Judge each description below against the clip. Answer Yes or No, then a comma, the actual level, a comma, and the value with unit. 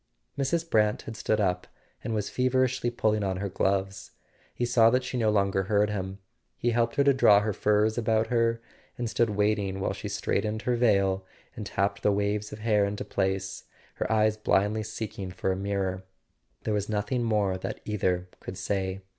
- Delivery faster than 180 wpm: Yes, average, 190 wpm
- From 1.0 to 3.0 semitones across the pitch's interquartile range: Yes, average, 2.7 semitones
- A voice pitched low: Yes, low, 105 Hz